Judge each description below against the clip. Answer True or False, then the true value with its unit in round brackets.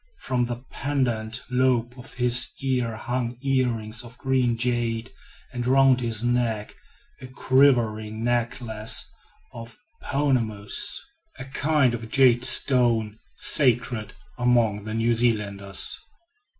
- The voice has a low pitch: True (120 Hz)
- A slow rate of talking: True (110 wpm)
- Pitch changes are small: True (2.3 semitones)